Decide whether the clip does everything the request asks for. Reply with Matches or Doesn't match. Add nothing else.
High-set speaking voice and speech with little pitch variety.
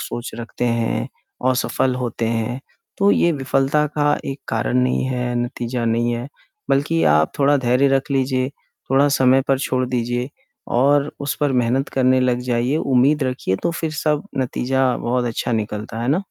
Doesn't match